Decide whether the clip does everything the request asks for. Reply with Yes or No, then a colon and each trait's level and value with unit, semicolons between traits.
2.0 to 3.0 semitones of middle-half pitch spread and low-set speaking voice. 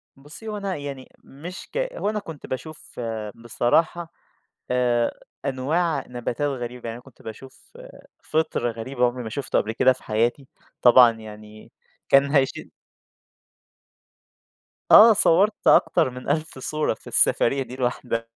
No: average, 4.6 semitones; low, 130 Hz